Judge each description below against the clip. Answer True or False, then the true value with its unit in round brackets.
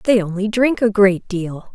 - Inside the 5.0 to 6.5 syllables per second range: False (4.2 syllables/s)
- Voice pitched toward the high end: True (205 Hz)